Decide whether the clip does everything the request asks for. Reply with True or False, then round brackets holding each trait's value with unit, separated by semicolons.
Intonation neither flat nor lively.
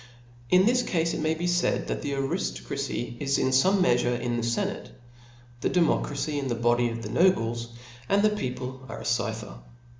False (6.4 semitones)